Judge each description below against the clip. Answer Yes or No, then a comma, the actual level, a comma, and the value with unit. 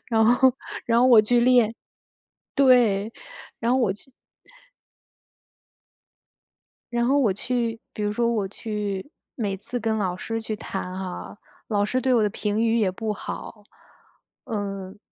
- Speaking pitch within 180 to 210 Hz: No, high, 220 Hz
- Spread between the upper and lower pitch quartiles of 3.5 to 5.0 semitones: No, average, 2.8 semitones